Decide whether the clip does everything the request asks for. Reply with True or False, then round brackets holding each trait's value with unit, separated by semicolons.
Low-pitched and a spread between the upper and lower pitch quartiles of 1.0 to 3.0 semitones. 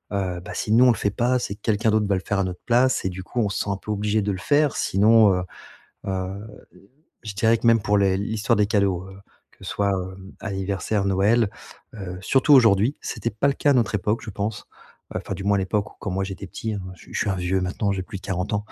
True (100 Hz; 2.5 semitones)